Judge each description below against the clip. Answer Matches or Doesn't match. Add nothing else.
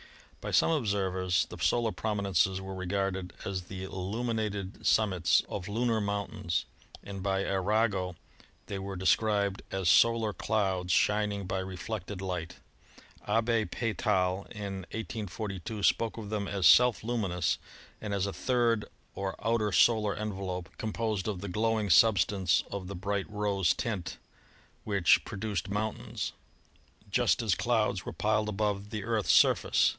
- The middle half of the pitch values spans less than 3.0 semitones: Matches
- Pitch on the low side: Matches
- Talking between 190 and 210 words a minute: Doesn't match